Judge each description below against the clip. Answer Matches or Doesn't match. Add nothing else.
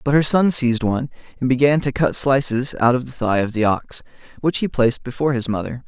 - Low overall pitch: Matches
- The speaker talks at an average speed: Doesn't match